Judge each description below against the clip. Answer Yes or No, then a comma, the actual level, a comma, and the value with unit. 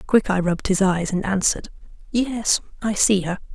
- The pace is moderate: Yes, average, 170 wpm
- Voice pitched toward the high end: Yes, high, 195 Hz